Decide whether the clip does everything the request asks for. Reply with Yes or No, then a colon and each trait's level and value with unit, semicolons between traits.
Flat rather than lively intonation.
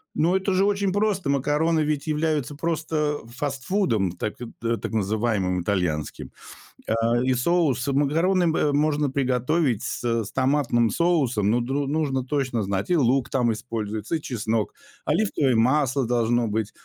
No: average, 5.1 semitones